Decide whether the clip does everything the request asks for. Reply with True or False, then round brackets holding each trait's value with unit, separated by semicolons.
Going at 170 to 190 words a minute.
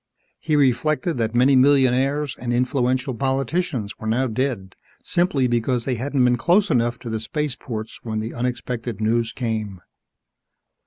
False (145 wpm)